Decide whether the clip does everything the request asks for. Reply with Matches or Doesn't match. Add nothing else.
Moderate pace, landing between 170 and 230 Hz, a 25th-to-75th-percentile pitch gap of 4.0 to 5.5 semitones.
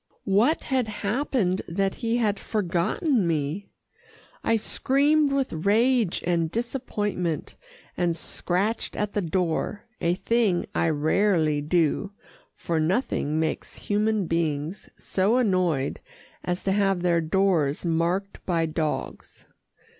Doesn't match